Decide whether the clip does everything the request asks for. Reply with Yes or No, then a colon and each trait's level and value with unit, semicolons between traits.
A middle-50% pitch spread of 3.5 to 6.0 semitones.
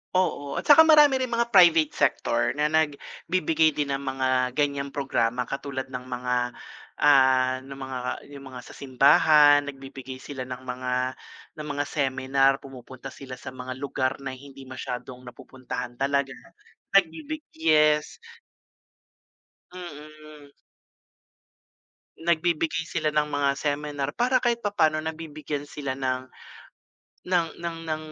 No: average, 3.0 semitones